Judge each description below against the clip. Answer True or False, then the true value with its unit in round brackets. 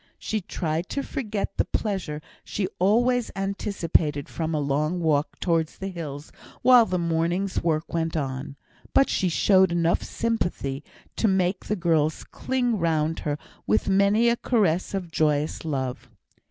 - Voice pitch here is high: False (170 Hz)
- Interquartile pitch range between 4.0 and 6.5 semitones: True (4.3 semitones)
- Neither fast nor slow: True (155 wpm)